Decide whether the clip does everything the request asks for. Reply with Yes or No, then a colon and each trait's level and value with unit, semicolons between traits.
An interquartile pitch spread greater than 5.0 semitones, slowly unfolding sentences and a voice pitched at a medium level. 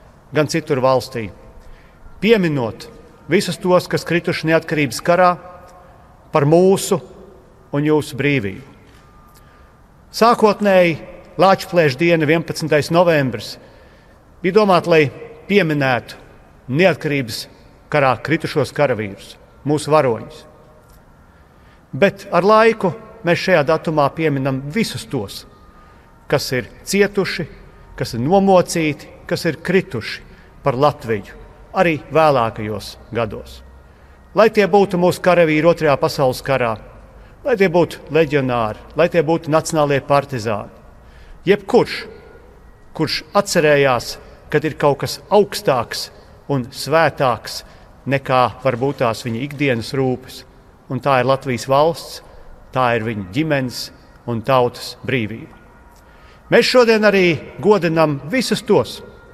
Yes: wide, 5.6 semitones; slow, 105 wpm; medium, 150 Hz